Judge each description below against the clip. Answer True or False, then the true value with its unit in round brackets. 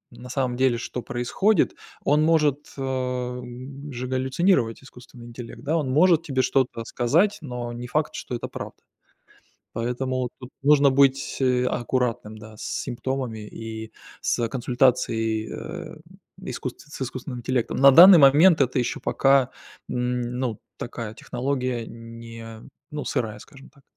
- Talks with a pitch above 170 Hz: False (125 Hz)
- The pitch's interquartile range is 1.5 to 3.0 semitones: True (2.5 semitones)